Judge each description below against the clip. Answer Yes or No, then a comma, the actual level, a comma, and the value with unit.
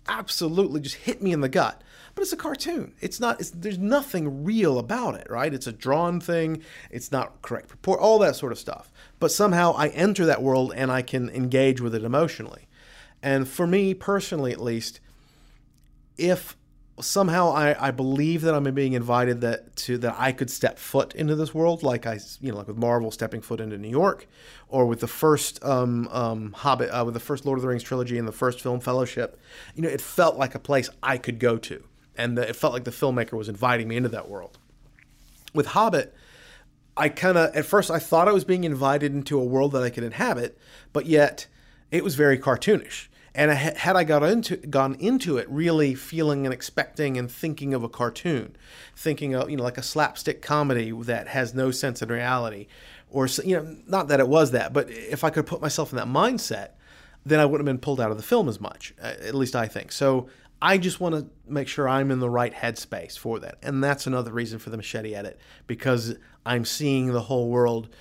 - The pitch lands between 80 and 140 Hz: Yes, low, 135 Hz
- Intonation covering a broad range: No, average, 4.4 semitones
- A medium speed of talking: No, fast, 215 wpm